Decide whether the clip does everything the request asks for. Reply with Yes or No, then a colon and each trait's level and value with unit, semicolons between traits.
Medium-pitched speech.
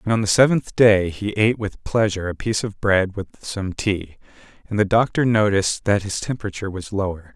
No: low, 105 Hz